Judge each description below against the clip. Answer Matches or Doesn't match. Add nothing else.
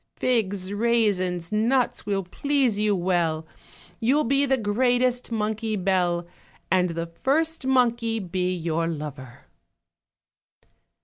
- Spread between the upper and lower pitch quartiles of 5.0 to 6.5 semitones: Matches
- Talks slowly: Matches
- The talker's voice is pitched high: Matches